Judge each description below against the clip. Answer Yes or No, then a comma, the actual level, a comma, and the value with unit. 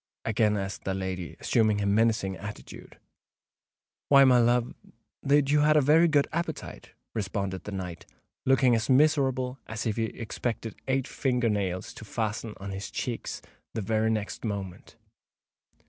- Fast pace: No, average, 145 wpm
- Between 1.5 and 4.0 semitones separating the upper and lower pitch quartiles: No, average, 4.6 semitones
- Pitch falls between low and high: No, low, 110 Hz